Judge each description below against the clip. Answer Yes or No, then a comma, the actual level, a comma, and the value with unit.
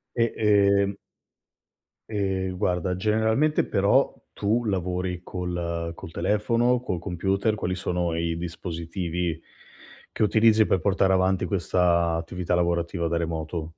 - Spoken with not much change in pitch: No, average, 3.0 semitones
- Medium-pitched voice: No, very low, 90 Hz